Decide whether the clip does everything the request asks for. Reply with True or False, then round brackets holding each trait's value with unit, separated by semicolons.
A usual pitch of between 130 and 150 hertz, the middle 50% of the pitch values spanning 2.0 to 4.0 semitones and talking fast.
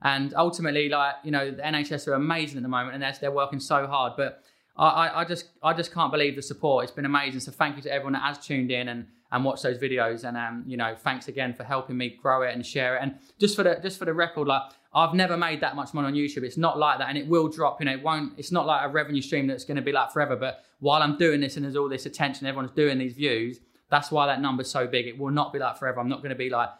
True (140 Hz; 2.6 semitones; 295 wpm)